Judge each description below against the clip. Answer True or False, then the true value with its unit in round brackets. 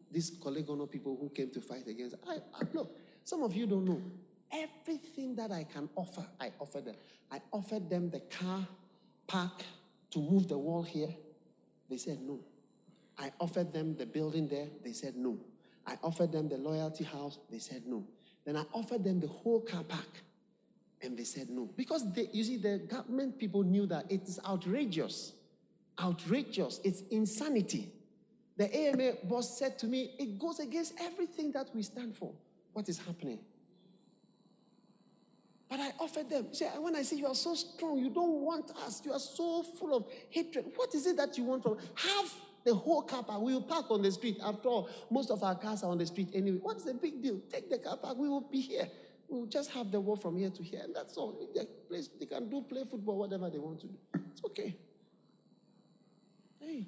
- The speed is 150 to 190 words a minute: False (200 wpm)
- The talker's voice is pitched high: True (210 Hz)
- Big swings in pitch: True (7.0 semitones)